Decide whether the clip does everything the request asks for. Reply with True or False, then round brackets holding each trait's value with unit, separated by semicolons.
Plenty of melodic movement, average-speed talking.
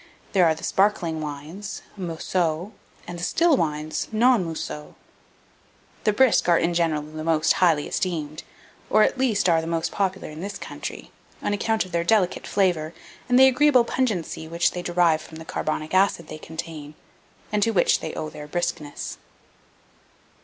False (4.3 semitones; 165 wpm)